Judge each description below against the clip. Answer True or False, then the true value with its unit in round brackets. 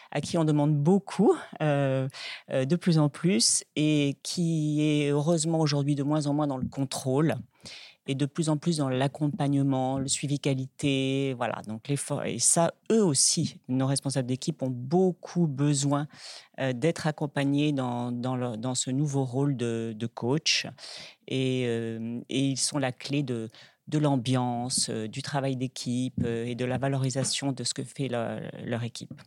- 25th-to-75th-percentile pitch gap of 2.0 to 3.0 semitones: True (2.7 semitones)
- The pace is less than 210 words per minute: True (175 wpm)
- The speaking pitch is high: False (140 Hz)